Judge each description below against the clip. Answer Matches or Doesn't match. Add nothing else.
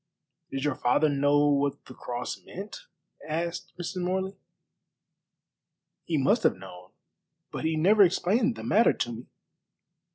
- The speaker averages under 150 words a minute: Matches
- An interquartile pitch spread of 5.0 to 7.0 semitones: Matches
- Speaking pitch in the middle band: Matches